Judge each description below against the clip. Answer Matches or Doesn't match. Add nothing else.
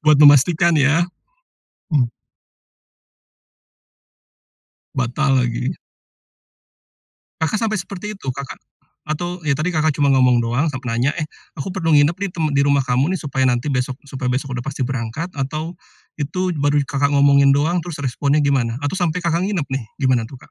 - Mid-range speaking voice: Matches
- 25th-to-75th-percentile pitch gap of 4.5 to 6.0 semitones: Doesn't match